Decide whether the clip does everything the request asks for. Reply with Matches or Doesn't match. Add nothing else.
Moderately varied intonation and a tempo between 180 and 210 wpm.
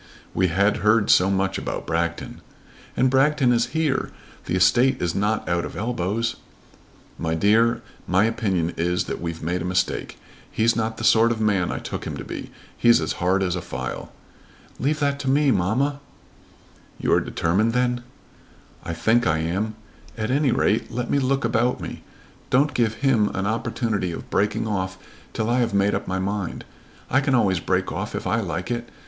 Matches